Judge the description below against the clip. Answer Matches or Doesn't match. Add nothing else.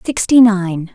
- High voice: Matches